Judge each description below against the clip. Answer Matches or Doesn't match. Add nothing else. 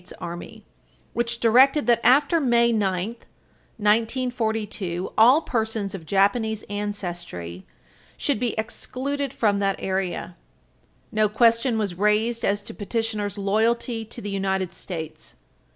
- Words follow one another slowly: Matches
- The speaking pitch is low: Doesn't match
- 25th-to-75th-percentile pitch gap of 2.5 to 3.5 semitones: Matches